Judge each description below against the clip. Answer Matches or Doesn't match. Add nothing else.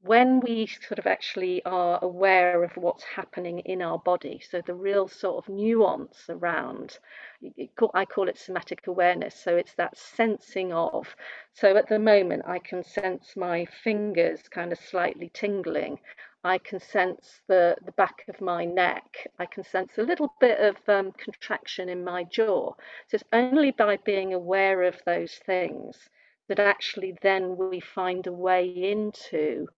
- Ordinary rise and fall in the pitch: Doesn't match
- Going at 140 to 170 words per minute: Matches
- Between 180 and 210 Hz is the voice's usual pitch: Matches